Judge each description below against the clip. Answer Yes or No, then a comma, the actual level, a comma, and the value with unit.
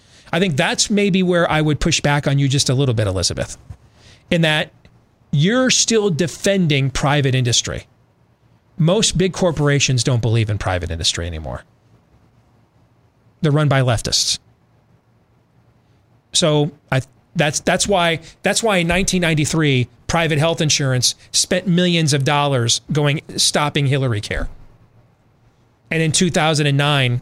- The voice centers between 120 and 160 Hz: Yes, medium, 140 Hz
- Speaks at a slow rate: Yes, slow, 130 wpm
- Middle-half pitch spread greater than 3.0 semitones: Yes, wide, 5.6 semitones